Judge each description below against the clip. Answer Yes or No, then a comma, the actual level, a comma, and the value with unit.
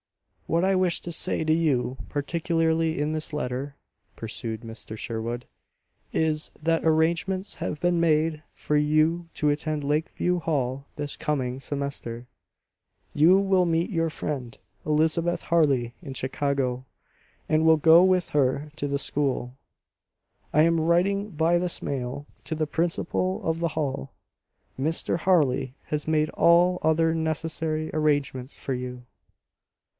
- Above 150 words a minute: No, slow, 135 wpm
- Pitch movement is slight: No, average, 3.0 semitones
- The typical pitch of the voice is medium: Yes, medium, 155 Hz